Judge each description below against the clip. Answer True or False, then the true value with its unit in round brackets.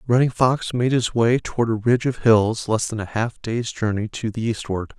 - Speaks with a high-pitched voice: False (115 Hz)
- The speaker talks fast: True (230 wpm)